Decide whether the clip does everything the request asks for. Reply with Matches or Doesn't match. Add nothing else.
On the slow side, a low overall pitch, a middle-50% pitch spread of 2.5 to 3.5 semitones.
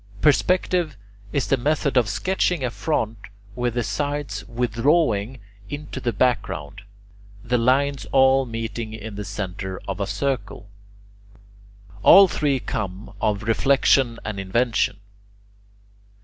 Doesn't match